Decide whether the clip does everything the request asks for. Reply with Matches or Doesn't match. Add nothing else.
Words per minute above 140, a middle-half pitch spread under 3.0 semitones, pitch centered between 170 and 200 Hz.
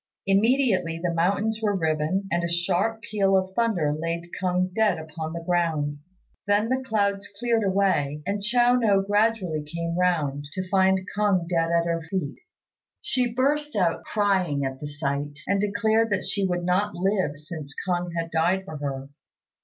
Doesn't match